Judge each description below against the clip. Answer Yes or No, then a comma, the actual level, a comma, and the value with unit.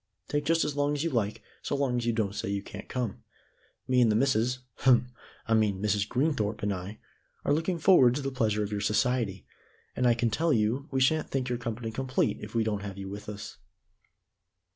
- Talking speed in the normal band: No, fast, 220 wpm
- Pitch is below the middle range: Yes, low, 120 Hz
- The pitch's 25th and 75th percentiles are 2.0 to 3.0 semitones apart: No, average, 4.1 semitones